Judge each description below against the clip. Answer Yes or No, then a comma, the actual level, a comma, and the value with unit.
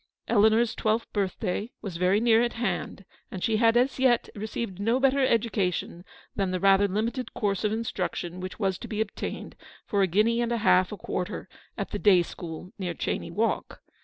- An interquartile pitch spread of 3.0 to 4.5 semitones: Yes, average, 3.7 semitones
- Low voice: No, high, 210 Hz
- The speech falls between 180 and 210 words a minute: Yes, average, 190 wpm